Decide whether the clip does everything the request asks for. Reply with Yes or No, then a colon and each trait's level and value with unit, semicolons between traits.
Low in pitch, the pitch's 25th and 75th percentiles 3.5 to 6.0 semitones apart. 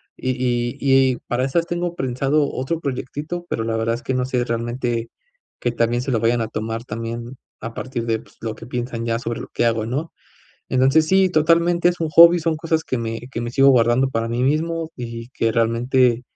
Yes: low, 125 Hz; average, 4.2 semitones